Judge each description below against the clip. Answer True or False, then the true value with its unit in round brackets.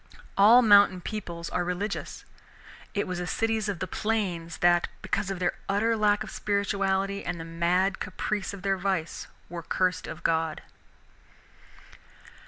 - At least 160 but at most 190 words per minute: False (150 wpm)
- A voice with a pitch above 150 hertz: True (190 Hz)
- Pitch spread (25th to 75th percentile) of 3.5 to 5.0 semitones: False (2.6 semitones)